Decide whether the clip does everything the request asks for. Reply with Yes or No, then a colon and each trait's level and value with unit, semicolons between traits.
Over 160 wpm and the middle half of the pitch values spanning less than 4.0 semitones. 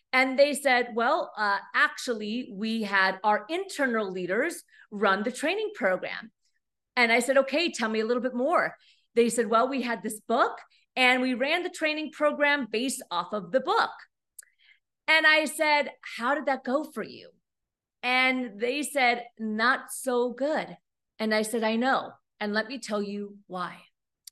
No: average, 170 wpm; average, 4.3 semitones